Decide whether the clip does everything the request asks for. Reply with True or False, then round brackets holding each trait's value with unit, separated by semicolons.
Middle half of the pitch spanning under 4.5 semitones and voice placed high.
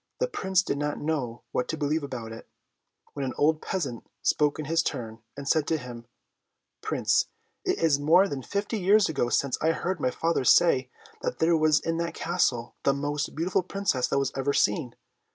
False (4.1 semitones; 150 Hz)